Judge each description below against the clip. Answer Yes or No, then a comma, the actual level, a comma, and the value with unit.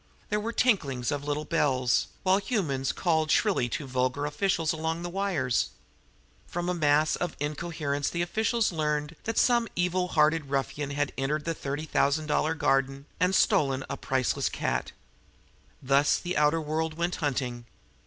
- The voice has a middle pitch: Yes, medium, 155 Hz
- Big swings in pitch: No, average, 3.8 semitones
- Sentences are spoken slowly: No, average, 160 wpm